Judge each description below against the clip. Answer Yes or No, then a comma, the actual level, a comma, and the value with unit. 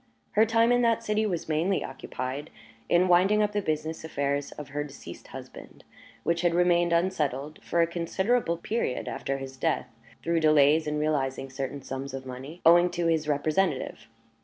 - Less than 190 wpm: Yes, average, 170 wpm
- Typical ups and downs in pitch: Yes, average, 4.1 semitones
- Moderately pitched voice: Yes, medium, 160 Hz